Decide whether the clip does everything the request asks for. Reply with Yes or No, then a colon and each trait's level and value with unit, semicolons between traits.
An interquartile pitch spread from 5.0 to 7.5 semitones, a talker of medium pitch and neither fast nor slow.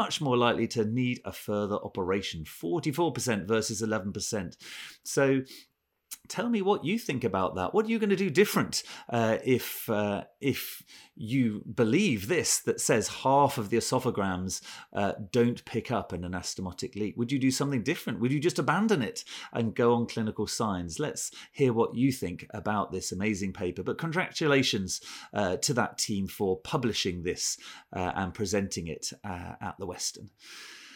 No: average, 5.3 semitones; low, 115 Hz; average, 170 wpm